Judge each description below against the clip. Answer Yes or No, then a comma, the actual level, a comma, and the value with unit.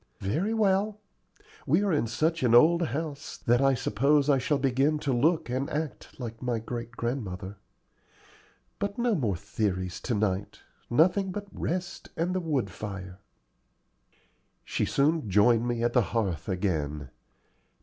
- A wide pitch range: Yes, wide, 7.2 semitones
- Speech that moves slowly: No, average, 150 wpm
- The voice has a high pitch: No, low, 125 Hz